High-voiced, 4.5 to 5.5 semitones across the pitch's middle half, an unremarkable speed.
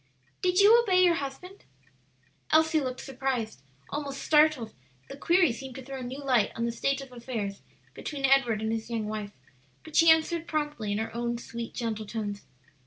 Yes: very high, 265 Hz; average, 5.2 semitones; average, 175 wpm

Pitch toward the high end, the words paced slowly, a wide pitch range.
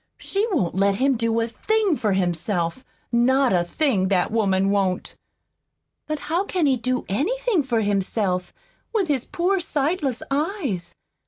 No: high, 240 Hz; average, 150 wpm; wide, 8.0 semitones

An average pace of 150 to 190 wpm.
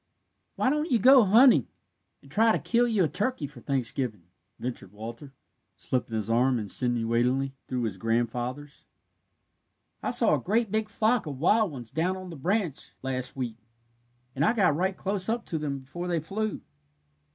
Yes: average, 170 wpm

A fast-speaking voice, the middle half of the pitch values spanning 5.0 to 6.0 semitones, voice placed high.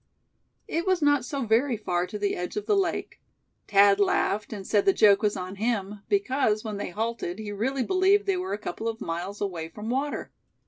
Yes: fast, 210 wpm; wide, 5.5 semitones; high, 215 Hz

